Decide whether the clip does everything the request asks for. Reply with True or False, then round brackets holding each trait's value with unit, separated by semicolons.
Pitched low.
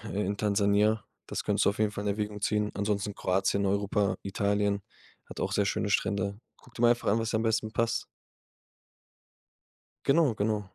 True (105 Hz)